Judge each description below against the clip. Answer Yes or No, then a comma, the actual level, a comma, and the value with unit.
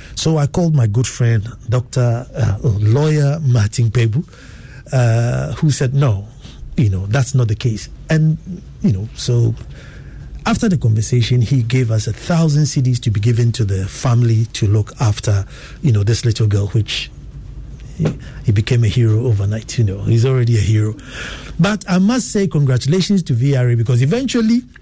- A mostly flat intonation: No, average, 4.0 semitones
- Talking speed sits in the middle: Yes, average, 170 wpm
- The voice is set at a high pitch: No, low, 125 Hz